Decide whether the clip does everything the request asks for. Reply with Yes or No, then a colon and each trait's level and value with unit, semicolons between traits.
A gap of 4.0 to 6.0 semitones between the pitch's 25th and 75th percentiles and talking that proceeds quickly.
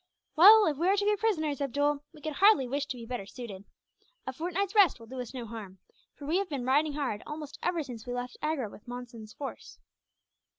Yes: average, 4.6 semitones; fast, 220 wpm